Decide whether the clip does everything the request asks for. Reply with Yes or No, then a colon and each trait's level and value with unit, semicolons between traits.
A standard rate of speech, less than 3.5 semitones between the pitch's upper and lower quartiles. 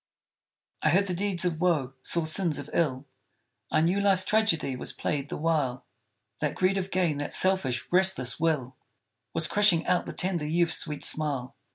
No: average, 175 wpm; average, 4.2 semitones